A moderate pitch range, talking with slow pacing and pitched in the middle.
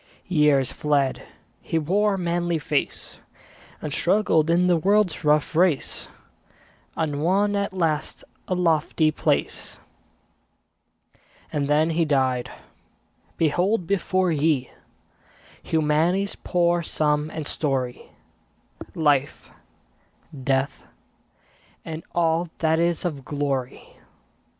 Yes: average, 3.0 semitones; slow, 100 wpm; medium, 160 Hz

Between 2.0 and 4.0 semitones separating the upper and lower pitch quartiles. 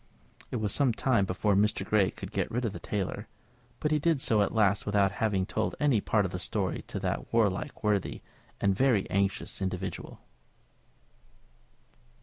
Yes: average, 2.8 semitones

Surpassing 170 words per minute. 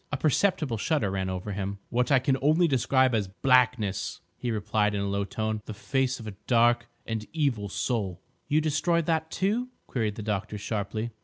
Yes: average, 180 wpm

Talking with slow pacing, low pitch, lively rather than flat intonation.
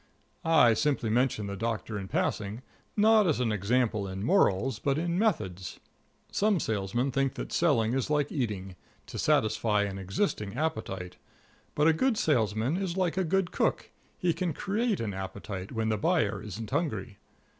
No: average, 165 wpm; low, 115 Hz; wide, 7.9 semitones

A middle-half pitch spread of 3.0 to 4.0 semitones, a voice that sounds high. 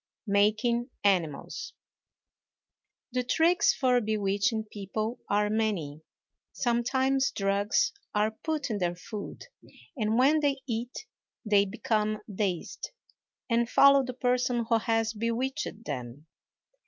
Yes: average, 3.6 semitones; high, 225 Hz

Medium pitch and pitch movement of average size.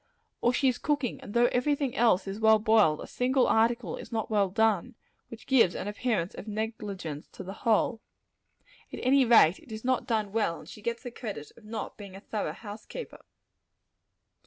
No: high, 220 Hz; average, 3.2 semitones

